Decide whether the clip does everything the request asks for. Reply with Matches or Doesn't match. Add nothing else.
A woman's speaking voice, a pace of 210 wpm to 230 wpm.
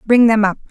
Doesn't match